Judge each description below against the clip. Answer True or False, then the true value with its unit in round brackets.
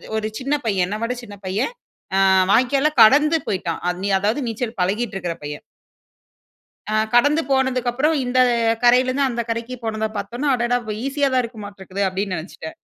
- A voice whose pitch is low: False (235 Hz)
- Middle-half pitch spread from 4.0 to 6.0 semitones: True (4.5 semitones)